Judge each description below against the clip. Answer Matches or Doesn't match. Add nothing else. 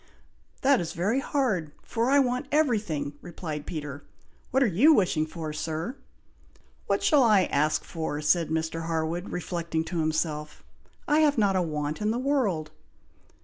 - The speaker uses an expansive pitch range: Matches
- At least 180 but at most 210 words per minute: Doesn't match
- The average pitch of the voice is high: Doesn't match